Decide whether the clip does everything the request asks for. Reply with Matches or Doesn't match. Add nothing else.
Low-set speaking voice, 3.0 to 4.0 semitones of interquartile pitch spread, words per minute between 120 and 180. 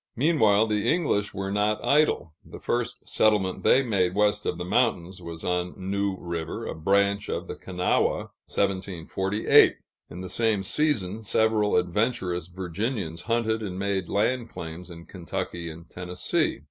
Matches